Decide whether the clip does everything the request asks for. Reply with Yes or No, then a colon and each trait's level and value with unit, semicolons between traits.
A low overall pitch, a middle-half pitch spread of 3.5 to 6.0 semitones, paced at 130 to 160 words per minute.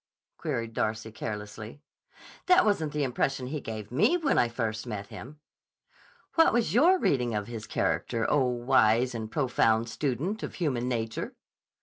Yes: low, 125 Hz; average, 5.1 semitones; average, 150 wpm